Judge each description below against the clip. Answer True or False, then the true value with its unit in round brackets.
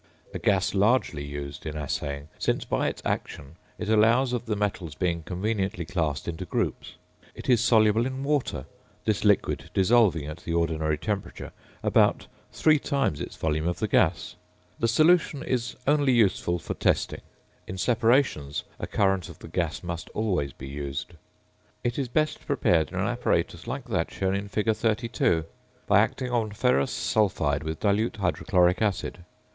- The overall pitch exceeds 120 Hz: False (95 Hz)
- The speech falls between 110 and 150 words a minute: False (160 wpm)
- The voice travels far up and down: True (6.4 semitones)